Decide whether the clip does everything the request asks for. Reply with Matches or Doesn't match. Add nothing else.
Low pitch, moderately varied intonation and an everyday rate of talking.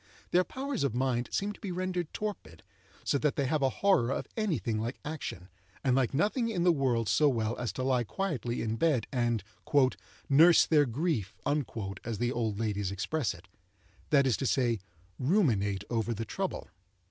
Doesn't match